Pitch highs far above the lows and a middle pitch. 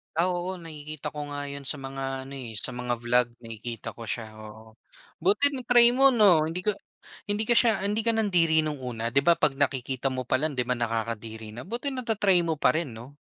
Yes: wide, 7.4 semitones; medium, 145 Hz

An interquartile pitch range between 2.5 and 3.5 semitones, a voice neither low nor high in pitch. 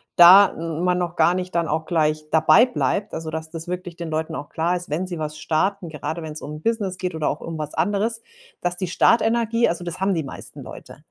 Yes: average, 2.9 semitones; medium, 170 Hz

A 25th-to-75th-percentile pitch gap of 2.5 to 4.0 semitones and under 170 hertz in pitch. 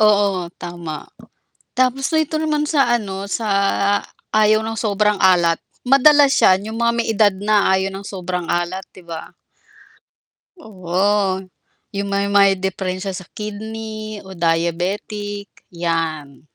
No: average, 3.1 semitones; high, 200 Hz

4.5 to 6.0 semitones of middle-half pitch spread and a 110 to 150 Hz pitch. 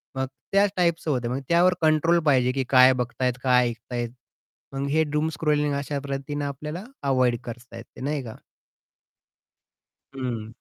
No: average, 3.3 semitones; low, 135 Hz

